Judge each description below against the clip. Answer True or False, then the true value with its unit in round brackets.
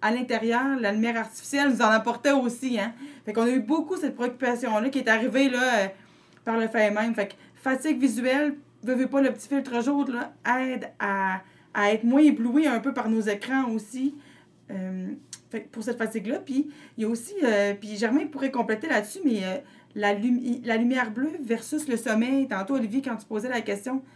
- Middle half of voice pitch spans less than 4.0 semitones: True (3.5 semitones)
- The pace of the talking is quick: False (205 wpm)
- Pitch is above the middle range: True (245 Hz)